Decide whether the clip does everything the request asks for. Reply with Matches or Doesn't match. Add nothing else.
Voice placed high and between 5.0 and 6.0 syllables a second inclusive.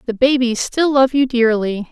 Doesn't match